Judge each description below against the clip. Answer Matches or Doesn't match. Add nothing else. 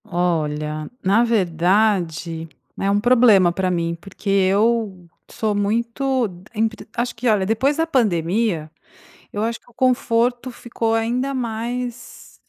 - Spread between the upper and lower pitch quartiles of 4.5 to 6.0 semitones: Matches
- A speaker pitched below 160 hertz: Doesn't match